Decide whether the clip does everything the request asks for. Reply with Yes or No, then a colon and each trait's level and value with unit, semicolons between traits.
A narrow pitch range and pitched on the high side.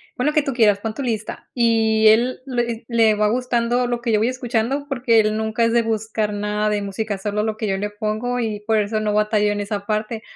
Yes: narrow, 2.1 semitones; high, 220 Hz